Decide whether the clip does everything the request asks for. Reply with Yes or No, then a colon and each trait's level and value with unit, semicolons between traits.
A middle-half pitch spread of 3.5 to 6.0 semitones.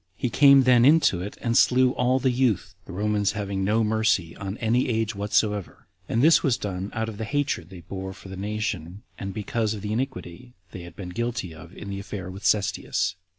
Yes: average, 3.9 semitones